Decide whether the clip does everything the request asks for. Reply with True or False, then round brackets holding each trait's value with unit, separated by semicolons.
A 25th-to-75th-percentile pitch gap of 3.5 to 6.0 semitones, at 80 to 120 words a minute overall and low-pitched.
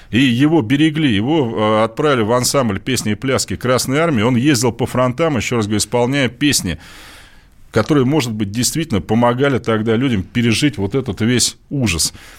False (4.3 semitones; 160 wpm; 120 Hz)